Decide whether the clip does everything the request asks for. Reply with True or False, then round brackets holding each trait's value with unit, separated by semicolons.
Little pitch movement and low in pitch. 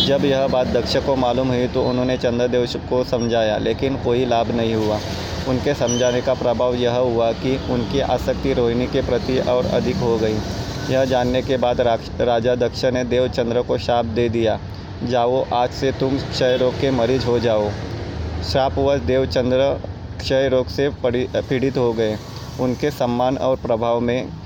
True (2.1 semitones; 125 Hz)